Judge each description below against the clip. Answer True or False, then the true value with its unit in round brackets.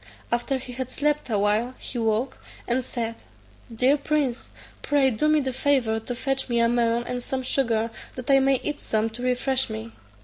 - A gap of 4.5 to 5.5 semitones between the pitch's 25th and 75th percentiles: False (2.7 semitones)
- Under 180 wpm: False (195 wpm)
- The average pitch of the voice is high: True (250 Hz)